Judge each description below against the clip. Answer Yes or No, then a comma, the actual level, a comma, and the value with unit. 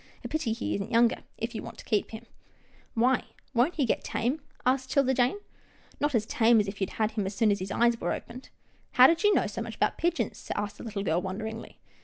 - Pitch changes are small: No, average, 3.2 semitones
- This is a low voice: No, high, 230 Hz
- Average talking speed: No, fast, 250 wpm